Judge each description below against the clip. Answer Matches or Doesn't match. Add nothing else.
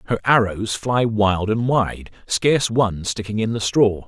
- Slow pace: Doesn't match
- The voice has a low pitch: Matches